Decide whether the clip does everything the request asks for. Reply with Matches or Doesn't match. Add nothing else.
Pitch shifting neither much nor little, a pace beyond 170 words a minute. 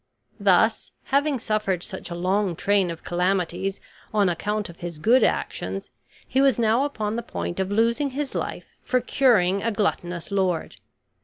Doesn't match